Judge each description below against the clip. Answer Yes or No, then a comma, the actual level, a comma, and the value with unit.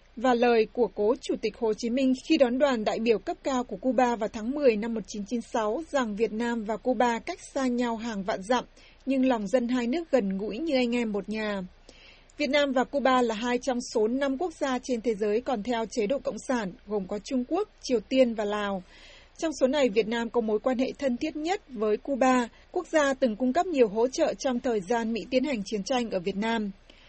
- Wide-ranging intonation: No, average, 3.1 semitones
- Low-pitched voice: No, high, 245 Hz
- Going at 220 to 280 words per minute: Yes, average, 235 wpm